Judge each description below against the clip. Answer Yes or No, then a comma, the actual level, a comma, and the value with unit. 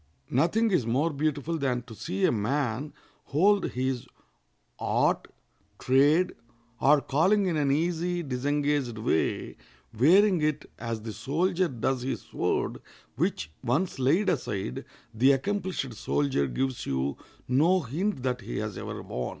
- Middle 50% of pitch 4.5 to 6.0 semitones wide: Yes, average, 5.3 semitones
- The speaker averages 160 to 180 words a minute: No, slow, 135 wpm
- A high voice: No, medium, 140 Hz